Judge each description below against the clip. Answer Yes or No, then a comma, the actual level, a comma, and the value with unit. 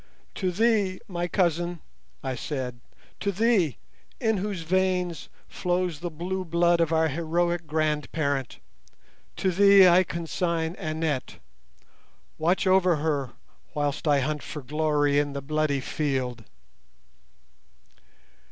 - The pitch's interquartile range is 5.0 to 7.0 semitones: No, average, 3.6 semitones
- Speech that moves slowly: Yes, slow, 115 wpm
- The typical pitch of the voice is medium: Yes, medium, 165 Hz